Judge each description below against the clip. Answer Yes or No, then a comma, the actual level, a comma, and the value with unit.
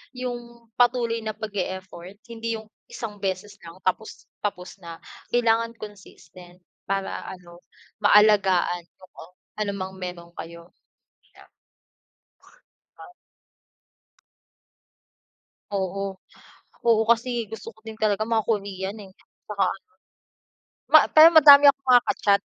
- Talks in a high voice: Yes, high, 205 Hz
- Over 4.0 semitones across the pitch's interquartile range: No, average, 3.6 semitones